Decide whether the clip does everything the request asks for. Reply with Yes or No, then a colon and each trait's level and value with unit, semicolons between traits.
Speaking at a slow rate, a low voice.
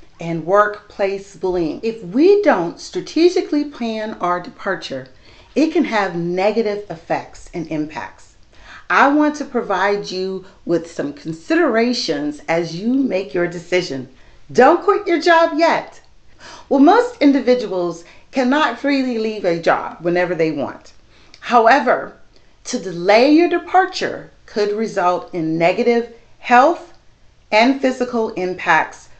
No: slow, 120 wpm; high, 215 Hz